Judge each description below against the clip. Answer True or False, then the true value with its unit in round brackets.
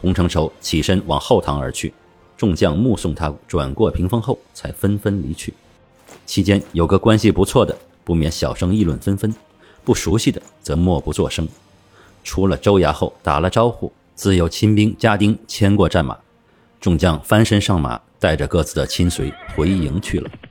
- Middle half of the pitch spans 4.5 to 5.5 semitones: False (4.1 semitones)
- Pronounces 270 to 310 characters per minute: False (255 characters per minute)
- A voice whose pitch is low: True (90 Hz)